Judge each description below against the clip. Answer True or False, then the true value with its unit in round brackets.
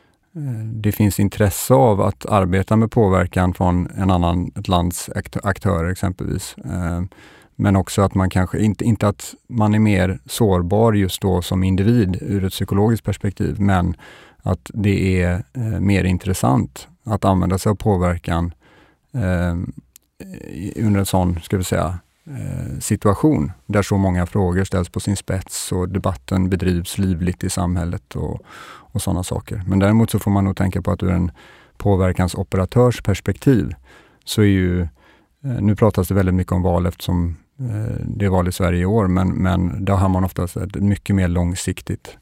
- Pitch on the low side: True (95 Hz)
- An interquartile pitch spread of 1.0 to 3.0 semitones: True (2.4 semitones)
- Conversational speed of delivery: True (160 wpm)